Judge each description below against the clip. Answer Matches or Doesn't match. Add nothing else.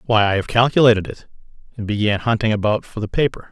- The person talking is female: Doesn't match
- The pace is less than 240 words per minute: Matches